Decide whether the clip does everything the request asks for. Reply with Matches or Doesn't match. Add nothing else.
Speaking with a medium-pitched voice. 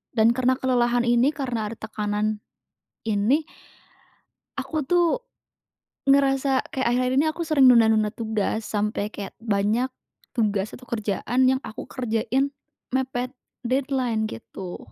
Doesn't match